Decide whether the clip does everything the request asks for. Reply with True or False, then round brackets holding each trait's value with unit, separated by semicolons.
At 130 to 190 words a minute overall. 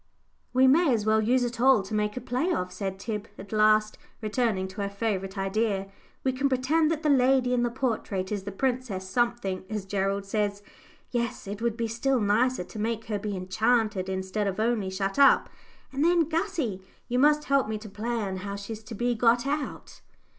False (200 wpm)